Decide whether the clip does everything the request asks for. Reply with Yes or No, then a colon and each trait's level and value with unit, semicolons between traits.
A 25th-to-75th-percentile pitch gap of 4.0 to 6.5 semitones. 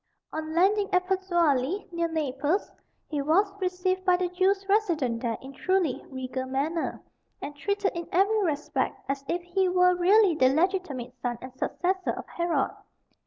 Yes: average, 5.1 semitones